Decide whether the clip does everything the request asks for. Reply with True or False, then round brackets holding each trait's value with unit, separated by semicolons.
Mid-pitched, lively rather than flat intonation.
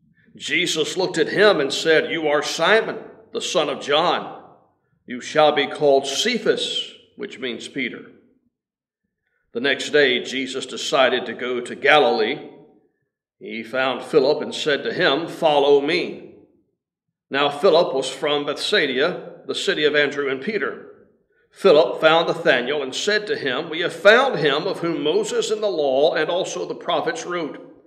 True (155 Hz; 7.6 semitones)